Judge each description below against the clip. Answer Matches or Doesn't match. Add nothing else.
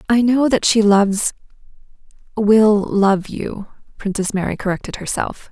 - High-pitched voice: Matches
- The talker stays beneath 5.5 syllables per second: Matches